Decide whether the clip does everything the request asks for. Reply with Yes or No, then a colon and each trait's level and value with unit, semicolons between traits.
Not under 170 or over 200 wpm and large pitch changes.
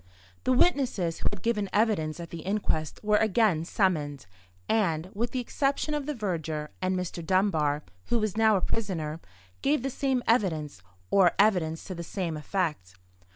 No: average, 155 wpm; wide, 5.7 semitones